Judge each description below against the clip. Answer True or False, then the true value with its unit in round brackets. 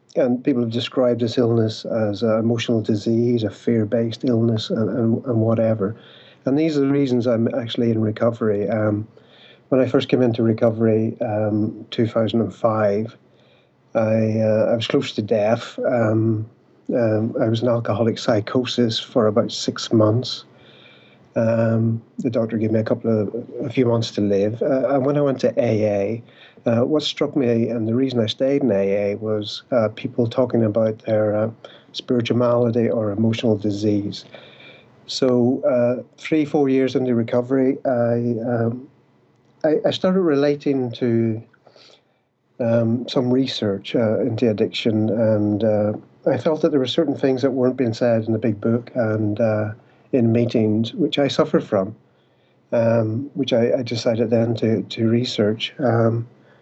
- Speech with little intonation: True (2.2 semitones)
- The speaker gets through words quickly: False (160 wpm)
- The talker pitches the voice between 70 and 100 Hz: False (115 Hz)